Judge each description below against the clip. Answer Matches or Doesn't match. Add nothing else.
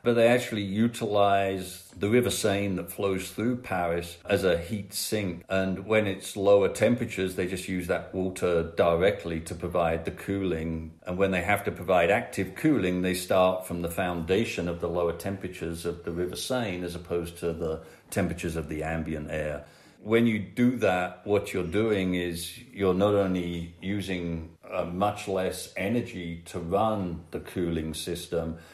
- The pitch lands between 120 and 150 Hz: Doesn't match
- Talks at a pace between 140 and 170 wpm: Matches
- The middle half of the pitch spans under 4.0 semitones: Matches